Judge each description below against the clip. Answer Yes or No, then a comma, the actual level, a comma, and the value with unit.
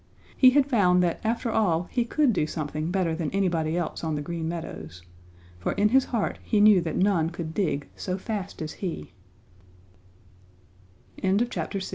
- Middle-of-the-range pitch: Yes, medium, 175 Hz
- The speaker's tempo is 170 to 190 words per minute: No, average, 140 wpm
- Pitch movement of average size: Yes, average, 4.9 semitones